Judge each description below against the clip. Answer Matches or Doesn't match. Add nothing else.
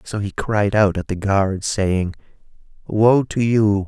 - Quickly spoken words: Doesn't match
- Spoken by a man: Matches